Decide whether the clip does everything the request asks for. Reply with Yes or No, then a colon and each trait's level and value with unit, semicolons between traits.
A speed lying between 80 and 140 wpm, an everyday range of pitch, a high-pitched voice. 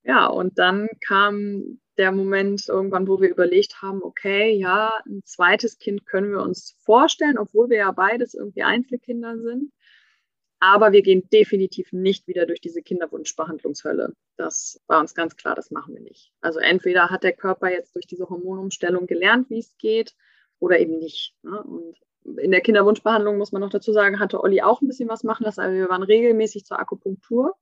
No: average, 185 wpm; average, 3.3 semitones; high, 200 Hz